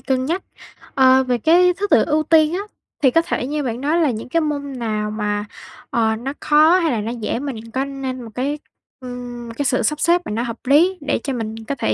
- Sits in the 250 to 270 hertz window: Yes, very high, 265 Hz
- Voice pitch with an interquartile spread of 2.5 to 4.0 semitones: No, average, 4.5 semitones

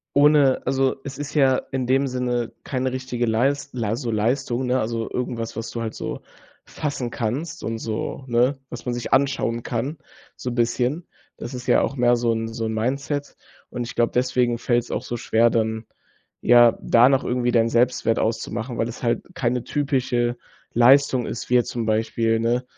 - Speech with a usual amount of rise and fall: No, narrow, 2.2 semitones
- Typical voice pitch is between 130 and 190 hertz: No, low, 120 Hz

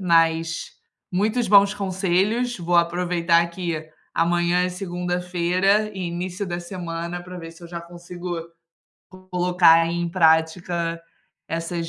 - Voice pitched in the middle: Yes, medium, 175 Hz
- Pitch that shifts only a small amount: Yes, narrow, 1.3 semitones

